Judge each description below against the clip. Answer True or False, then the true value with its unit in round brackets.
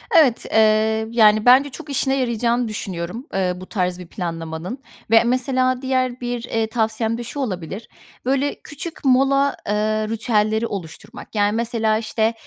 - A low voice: False (225 Hz)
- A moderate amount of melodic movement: True (3.3 semitones)